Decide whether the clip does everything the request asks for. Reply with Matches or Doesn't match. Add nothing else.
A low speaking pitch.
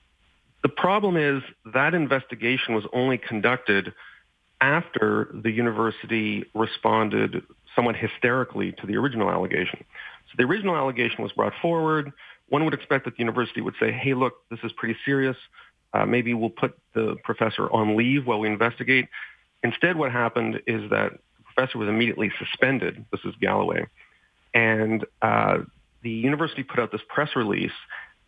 Matches